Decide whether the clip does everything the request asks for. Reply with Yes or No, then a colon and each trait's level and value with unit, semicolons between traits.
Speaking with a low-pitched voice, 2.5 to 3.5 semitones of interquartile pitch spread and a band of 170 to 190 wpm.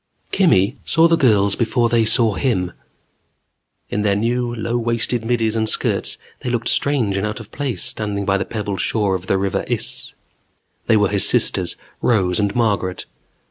Yes: low, 110 Hz; average, 3.1 semitones; average, 175 wpm